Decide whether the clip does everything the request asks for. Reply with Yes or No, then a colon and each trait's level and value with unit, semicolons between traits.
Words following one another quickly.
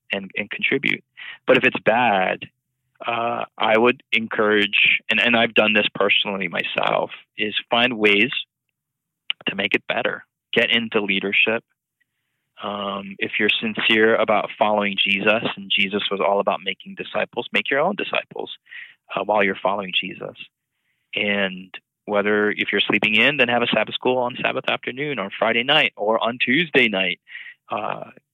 No: average, 155 wpm